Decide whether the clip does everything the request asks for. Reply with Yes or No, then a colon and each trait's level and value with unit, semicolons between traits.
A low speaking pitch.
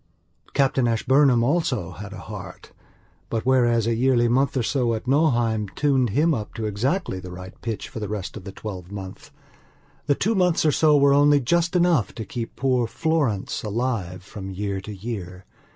Yes: low, 120 Hz